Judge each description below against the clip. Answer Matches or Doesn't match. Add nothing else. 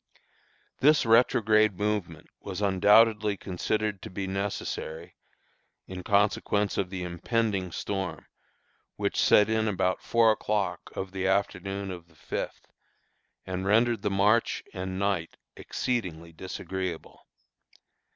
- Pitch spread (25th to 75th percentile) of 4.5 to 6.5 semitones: Doesn't match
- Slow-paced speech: Matches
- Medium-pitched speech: Doesn't match